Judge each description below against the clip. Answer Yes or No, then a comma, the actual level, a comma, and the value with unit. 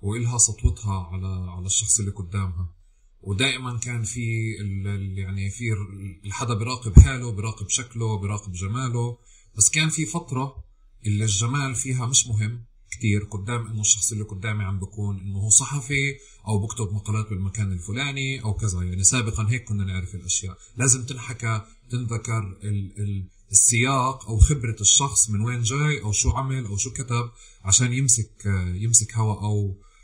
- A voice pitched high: No, low, 110 Hz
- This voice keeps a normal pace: No, fast, 150 wpm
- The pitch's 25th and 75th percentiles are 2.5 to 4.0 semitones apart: Yes, average, 3.4 semitones